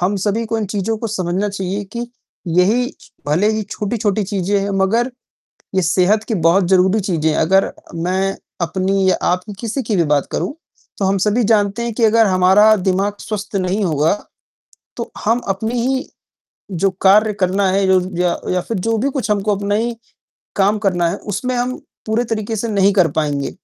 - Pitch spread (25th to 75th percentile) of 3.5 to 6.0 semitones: No, average, 2.8 semitones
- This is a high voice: Yes, high, 200 Hz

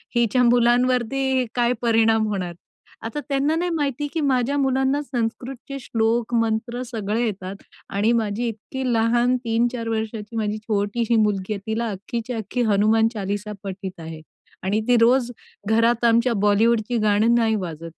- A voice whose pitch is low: No, high, 230 Hz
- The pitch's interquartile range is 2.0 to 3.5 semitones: Yes, narrow, 2.5 semitones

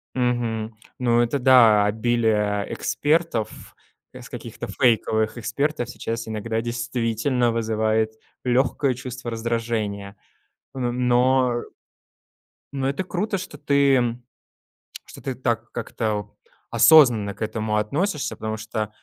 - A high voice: No, low, 120 Hz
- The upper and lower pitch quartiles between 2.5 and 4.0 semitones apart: Yes, average, 2.8 semitones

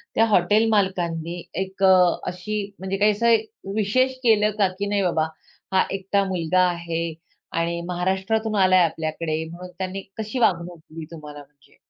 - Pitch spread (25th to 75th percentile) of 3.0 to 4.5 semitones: Yes, average, 3.5 semitones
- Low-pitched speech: No, medium, 185 Hz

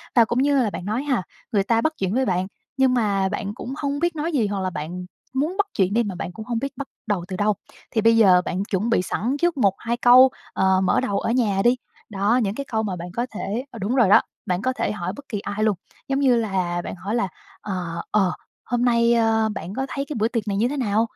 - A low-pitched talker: No, high, 220 Hz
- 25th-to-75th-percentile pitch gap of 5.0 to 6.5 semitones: No, average, 4.4 semitones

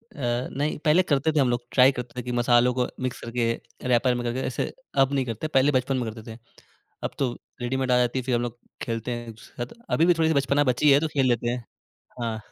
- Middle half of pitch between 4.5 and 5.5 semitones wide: No, narrow, 2.5 semitones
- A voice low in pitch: Yes, low, 125 Hz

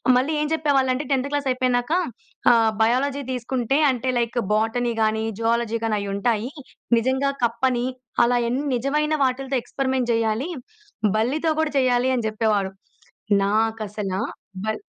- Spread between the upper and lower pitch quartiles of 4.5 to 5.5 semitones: No, average, 3.0 semitones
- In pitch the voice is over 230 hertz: Yes, high, 245 Hz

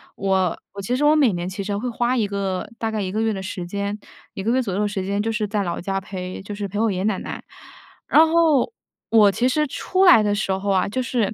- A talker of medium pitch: No, high, 205 Hz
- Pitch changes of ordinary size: Yes, average, 3.4 semitones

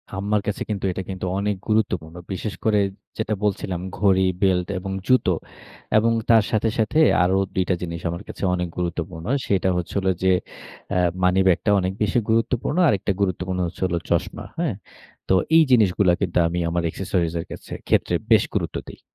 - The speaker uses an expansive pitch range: No, average, 2.8 semitones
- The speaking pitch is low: Yes, very low, 95 Hz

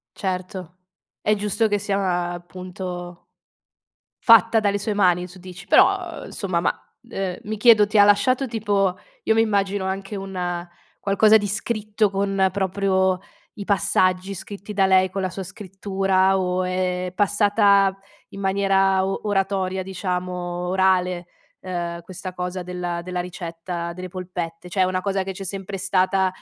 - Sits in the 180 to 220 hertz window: Yes, high, 190 Hz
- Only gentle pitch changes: Yes, narrow, 1.8 semitones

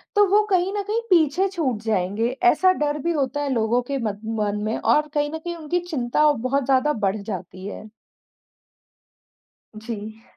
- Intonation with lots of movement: Yes, wide, 7.2 semitones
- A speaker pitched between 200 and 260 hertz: No, very high, 280 Hz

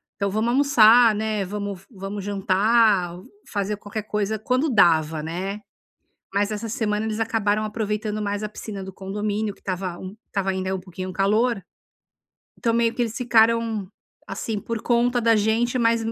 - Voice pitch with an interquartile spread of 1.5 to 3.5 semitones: Yes, narrow, 2.6 semitones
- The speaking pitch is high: Yes, high, 210 Hz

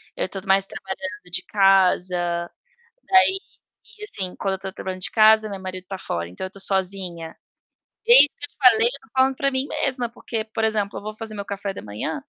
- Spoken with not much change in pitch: No, average, 3.3 semitones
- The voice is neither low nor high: No, high, 200 Hz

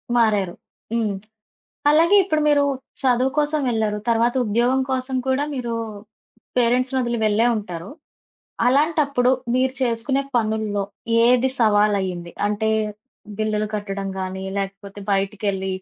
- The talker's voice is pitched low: No, high, 230 Hz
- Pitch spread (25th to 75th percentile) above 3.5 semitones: Yes, average, 4.1 semitones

